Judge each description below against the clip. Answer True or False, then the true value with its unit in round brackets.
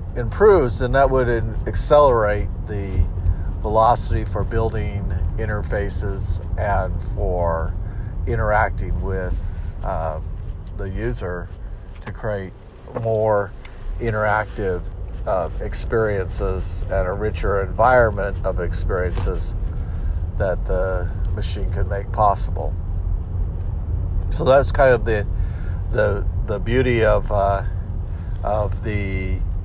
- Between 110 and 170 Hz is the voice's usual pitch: False (95 Hz)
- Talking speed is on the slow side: True (95 wpm)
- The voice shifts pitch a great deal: False (2.8 semitones)